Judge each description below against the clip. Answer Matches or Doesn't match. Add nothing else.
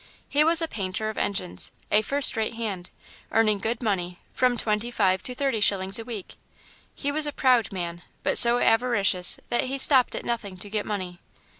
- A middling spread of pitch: Matches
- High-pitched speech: Matches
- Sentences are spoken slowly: Doesn't match